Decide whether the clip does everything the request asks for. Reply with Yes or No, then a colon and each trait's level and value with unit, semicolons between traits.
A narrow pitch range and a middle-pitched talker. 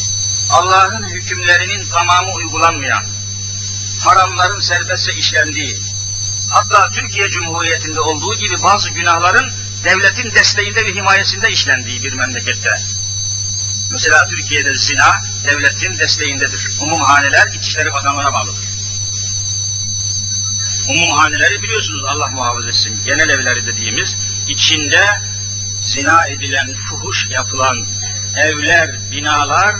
No: narrow, 1.1 semitones; low, 100 Hz